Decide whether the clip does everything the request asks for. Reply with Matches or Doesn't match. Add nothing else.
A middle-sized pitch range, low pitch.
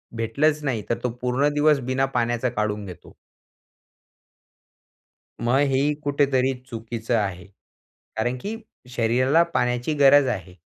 Matches